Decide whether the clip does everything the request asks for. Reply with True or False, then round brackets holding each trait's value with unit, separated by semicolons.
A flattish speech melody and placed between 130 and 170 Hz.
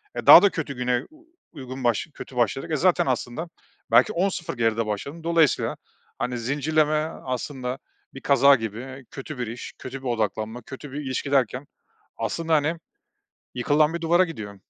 False (4.2 semitones; 135 Hz)